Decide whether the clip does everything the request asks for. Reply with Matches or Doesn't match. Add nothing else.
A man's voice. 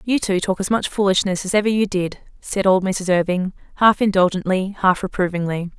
Doesn't match